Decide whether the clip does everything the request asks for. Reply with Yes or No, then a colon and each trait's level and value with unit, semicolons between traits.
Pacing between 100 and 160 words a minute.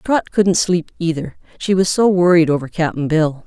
No: average, 190 wpm